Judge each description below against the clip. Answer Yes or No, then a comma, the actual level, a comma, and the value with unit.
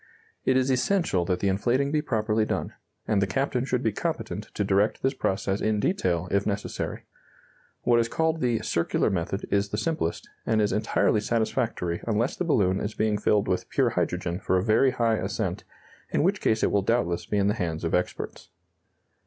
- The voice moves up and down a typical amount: Yes, average, 4.0 semitones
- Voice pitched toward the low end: Yes, low, 105 Hz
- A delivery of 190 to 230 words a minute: Yes, average, 195 wpm